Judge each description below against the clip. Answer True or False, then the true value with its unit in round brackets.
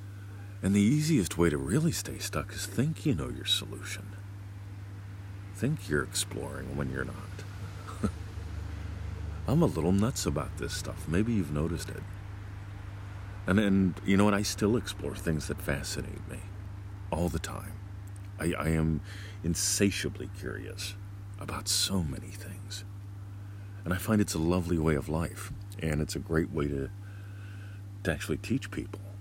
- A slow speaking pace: False (150 wpm)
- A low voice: True (100 Hz)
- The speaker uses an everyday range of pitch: False (1.7 semitones)